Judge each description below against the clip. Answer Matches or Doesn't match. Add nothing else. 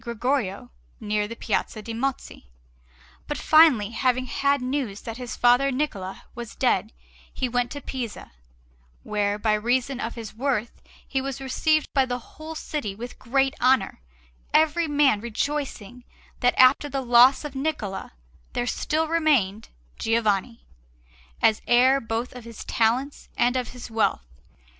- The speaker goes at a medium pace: Matches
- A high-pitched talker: Matches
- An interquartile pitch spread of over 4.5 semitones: Doesn't match